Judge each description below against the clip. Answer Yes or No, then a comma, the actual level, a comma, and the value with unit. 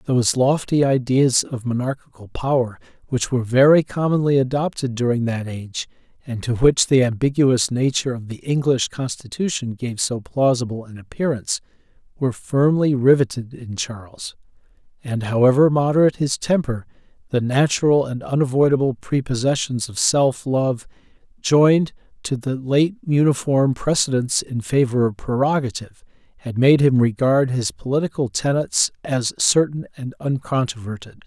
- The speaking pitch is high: No, low, 130 Hz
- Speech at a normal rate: No, slow, 130 wpm